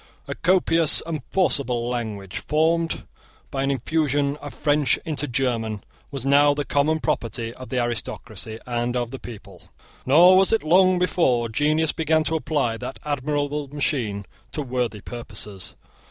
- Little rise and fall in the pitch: No, average, 4.5 semitones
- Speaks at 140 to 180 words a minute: Yes, average, 150 wpm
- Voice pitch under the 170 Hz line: Yes, medium, 140 Hz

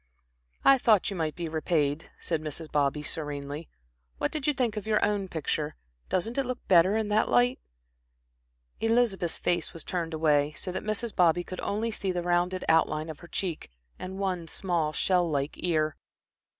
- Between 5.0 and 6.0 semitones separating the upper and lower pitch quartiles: No, average, 4.5 semitones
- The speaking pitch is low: No, medium, 175 Hz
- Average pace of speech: Yes, average, 175 wpm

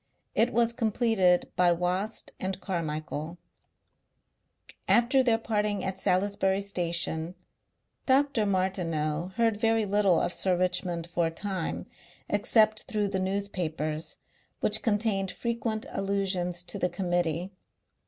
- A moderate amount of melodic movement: Yes, average, 3.4 semitones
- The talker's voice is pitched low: No, high, 190 Hz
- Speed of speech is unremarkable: No, slow, 115 wpm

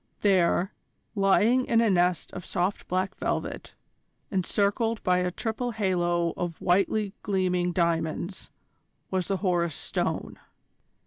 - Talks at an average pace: No, slow, 120 wpm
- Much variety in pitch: No, narrow, 2.5 semitones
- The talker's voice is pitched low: No, medium, 185 Hz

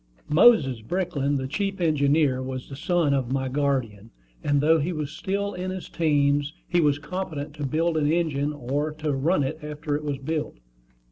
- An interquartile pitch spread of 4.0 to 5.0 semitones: No, average, 2.7 semitones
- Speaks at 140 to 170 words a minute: No, average, 185 wpm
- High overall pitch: No, medium, 150 Hz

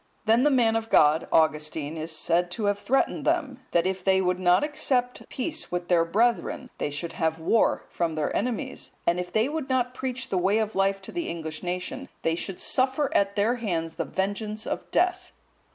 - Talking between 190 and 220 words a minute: Yes, average, 200 wpm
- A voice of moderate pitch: No, high, 200 Hz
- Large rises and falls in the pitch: Yes, wide, 6.5 semitones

